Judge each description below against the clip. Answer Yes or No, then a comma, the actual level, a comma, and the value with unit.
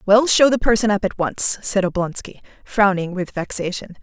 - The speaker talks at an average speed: Yes, average, 180 wpm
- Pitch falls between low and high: No, high, 200 Hz